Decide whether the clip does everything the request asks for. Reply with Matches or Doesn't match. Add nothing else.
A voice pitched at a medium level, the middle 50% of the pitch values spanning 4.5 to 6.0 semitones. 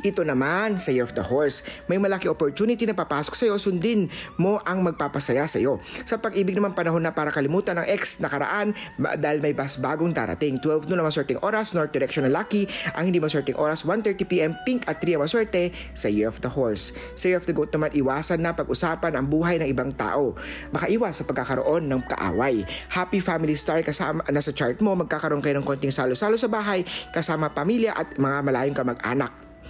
Matches